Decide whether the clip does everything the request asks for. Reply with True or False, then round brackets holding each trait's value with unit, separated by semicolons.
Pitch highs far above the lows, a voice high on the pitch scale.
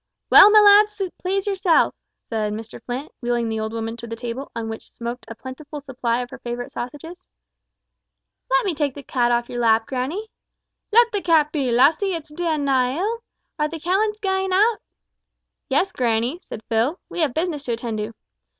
True (7.4 semitones; 280 Hz)